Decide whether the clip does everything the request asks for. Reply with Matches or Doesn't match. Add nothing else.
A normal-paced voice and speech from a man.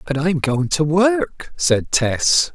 Matches